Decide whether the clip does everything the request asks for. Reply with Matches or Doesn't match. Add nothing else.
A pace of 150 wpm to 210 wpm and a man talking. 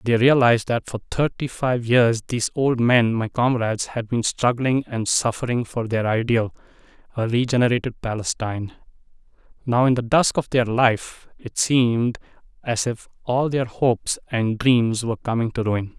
Matches